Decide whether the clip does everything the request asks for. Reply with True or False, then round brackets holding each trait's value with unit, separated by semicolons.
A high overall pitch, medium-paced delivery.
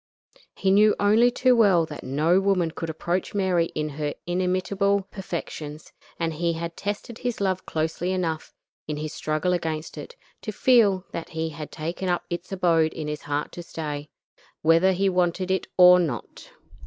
False (175 Hz; 170 wpm)